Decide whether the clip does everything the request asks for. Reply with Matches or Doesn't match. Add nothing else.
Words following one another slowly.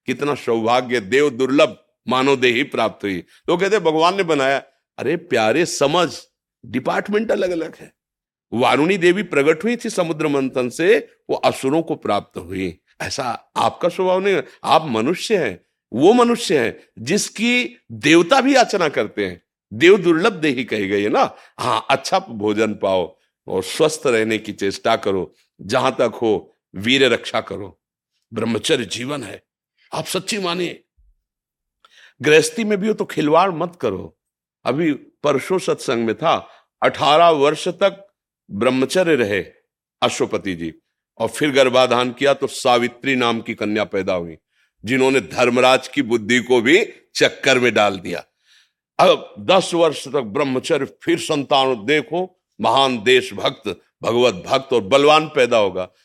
Doesn't match